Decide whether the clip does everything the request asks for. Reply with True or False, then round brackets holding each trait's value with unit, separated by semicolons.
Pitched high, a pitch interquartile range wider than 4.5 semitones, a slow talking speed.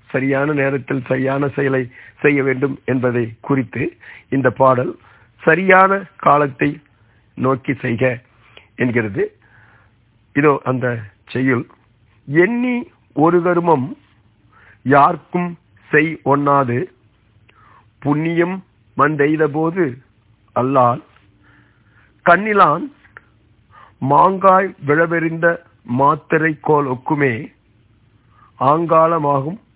False (135 Hz; 5.0 semitones; 65 wpm)